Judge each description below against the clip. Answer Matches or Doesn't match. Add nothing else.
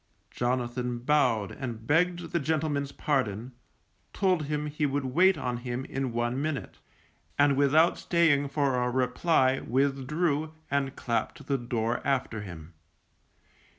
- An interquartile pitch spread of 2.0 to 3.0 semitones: Doesn't match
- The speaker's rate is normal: Doesn't match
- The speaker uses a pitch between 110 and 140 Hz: Matches